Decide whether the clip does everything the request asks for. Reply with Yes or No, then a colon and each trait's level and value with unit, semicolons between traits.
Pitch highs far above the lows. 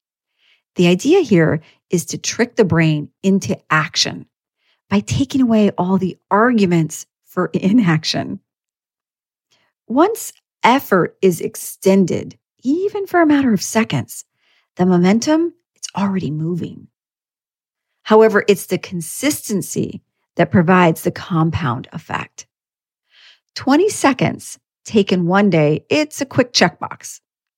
Yes: wide, 5.7 semitones